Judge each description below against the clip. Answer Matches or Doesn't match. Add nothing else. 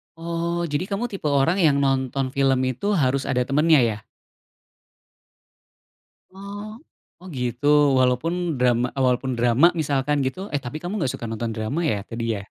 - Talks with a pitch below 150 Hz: Matches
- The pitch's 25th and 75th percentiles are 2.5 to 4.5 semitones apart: Doesn't match